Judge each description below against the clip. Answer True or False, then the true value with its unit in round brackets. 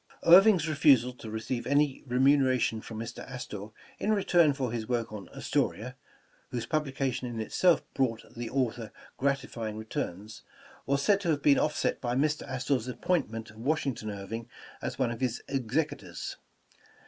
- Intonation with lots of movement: False (3.9 semitones)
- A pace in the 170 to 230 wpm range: False (160 wpm)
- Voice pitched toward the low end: True (125 Hz)